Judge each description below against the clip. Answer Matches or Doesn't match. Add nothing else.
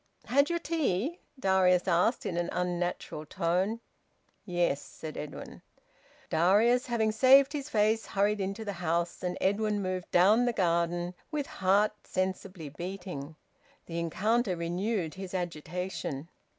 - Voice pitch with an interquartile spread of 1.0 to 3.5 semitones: Doesn't match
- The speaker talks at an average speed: Doesn't match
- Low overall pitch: Doesn't match